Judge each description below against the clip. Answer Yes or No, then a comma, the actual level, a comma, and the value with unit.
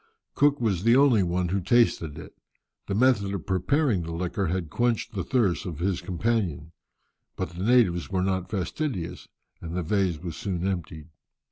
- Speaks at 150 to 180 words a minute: Yes, average, 170 wpm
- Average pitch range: Yes, average, 4.5 semitones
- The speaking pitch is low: Yes, very low, 95 Hz